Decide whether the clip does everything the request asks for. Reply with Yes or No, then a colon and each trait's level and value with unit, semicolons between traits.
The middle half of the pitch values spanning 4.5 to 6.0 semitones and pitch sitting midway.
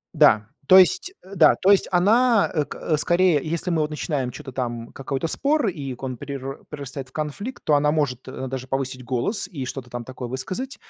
Yes: wide, 5.6 semitones; medium, 145 Hz